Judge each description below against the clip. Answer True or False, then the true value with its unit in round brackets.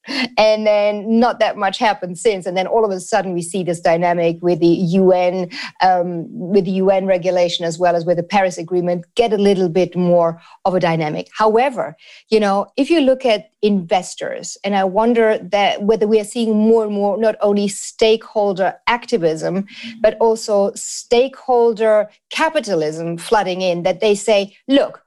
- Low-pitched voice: False (205 Hz)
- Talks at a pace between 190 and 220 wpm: False (175 wpm)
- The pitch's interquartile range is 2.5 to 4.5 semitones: True (3.6 semitones)